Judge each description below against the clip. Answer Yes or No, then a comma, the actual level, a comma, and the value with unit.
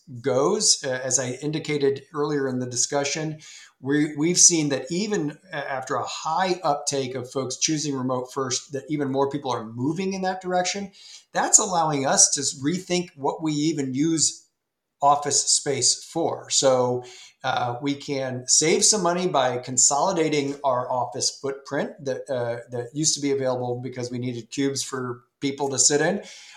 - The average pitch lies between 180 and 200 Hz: No, medium, 140 Hz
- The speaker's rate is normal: Yes, average, 165 wpm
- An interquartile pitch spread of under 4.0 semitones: Yes, average, 3.5 semitones